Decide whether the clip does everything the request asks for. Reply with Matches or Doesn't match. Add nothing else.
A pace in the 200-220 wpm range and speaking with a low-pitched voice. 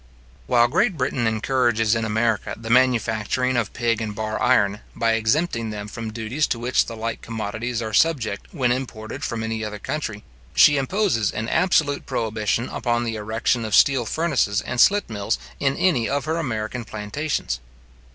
Doesn't match